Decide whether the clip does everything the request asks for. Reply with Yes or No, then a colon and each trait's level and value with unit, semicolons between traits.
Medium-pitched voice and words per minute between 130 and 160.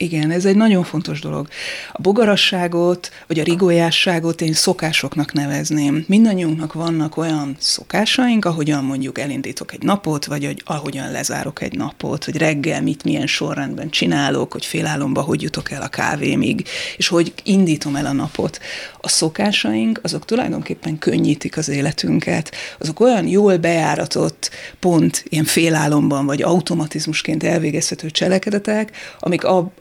Yes: medium, 165 Hz; average, 135 wpm